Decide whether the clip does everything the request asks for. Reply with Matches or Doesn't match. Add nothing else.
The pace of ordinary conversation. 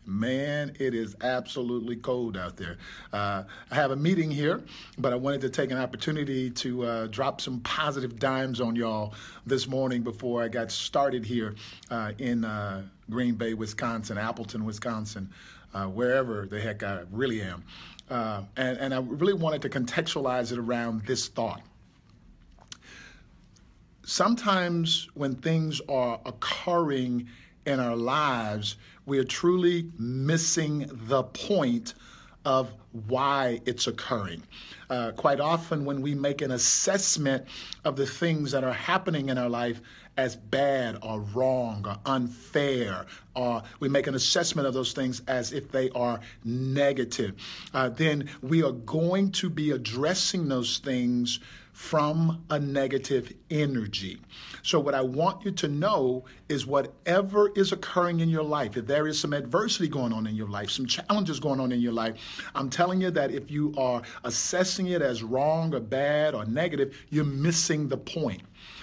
Matches